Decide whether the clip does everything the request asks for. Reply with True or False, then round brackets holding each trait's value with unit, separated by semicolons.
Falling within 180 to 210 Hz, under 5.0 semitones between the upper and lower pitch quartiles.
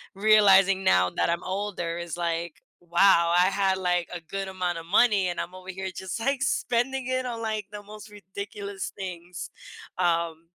True (190 Hz; 3.1 semitones)